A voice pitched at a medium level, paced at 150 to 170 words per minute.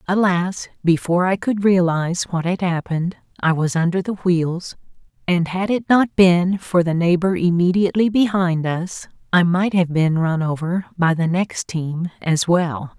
Yes: medium, 175 Hz; average, 165 wpm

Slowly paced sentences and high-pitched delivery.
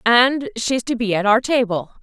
No: fast, 210 wpm; high, 240 Hz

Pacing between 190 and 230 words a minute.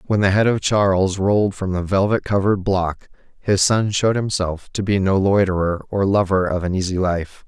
Yes: average, 200 wpm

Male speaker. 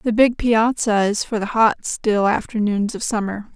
No: female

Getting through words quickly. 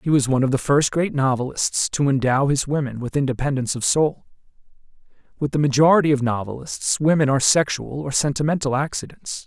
No: average, 170 wpm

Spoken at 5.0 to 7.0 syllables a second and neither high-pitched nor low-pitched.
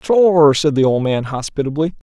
Yes: 5.3 syllables/s; medium, 150 Hz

